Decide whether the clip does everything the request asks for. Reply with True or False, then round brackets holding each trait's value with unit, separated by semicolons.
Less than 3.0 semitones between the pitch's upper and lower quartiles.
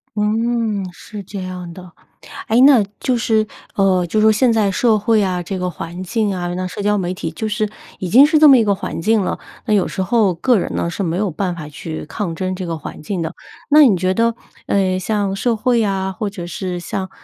False (3.3 semitones)